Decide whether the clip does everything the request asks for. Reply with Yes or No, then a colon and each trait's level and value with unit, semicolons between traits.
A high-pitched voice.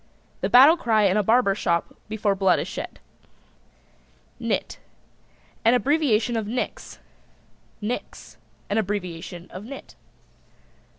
Yes: high, 215 Hz